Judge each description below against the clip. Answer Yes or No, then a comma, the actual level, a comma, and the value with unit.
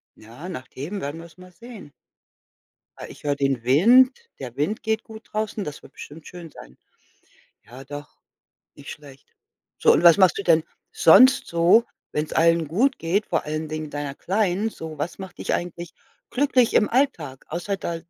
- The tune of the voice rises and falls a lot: Yes, wide, 5.8 semitones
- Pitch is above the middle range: No, medium, 170 Hz